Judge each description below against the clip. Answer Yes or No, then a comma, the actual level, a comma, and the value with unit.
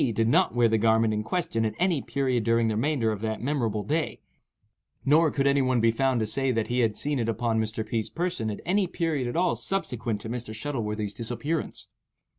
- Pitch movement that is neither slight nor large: Yes, average, 4.2 semitones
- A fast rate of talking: Yes, fast, 215 wpm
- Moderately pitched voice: No, low, 120 Hz